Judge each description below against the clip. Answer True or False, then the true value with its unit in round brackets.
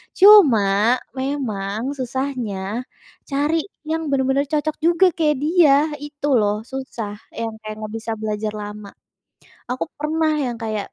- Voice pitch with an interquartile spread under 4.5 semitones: False (5.6 semitones)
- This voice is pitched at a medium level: False (260 Hz)